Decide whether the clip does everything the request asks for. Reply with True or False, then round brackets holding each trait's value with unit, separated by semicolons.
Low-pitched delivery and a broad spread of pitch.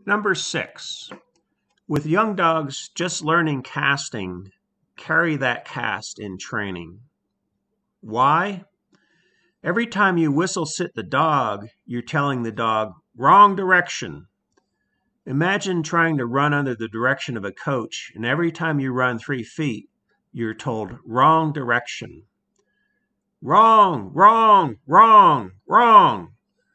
False (150 Hz; 7.9 semitones)